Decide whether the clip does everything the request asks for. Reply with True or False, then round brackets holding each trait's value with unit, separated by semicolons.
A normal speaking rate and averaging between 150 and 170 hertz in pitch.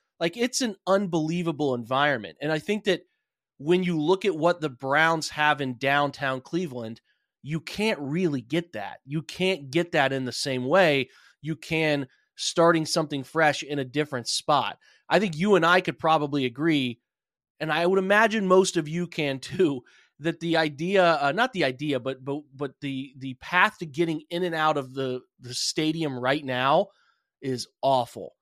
True (180 wpm; 155 Hz)